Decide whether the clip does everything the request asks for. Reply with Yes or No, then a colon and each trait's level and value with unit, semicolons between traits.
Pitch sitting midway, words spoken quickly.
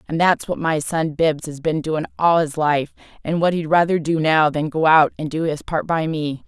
Yes: medium, 160 Hz; fast, 250 wpm